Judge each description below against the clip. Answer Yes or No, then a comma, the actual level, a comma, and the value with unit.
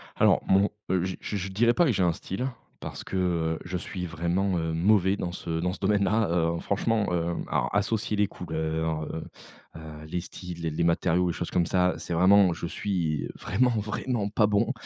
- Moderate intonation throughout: Yes, average, 3.4 semitones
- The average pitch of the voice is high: No, very low, 90 Hz